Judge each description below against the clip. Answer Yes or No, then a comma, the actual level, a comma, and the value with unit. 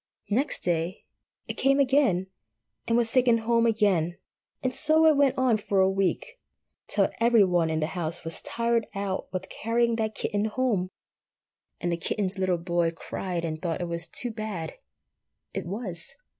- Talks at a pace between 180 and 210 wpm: No, average, 170 wpm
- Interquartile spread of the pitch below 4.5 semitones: No, average, 5.1 semitones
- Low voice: No, high, 205 Hz